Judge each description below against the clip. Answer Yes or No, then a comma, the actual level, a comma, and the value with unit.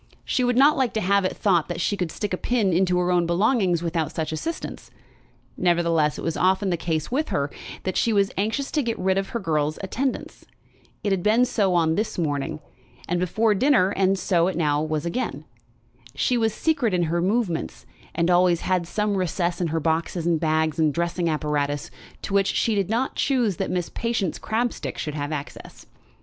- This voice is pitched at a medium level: Yes, medium, 180 Hz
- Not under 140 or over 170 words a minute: No, average, 200 wpm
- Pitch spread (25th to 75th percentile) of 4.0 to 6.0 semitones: Yes, average, 4.5 semitones